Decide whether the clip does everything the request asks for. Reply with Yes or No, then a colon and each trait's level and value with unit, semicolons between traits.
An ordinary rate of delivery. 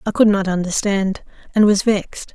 Yes: average, 180 wpm